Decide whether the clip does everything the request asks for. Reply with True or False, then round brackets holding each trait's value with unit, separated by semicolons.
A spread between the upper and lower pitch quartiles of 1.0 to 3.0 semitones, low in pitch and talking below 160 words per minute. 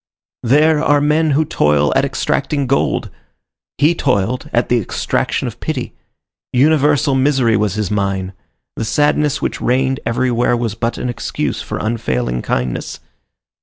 False (5.4 semitones; 125 Hz; 140 wpm)